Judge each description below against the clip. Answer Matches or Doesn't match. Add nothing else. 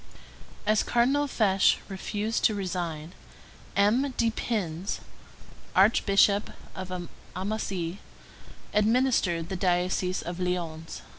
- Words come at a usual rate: Doesn't match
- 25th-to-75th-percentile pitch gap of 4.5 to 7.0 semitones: Doesn't match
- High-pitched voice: Matches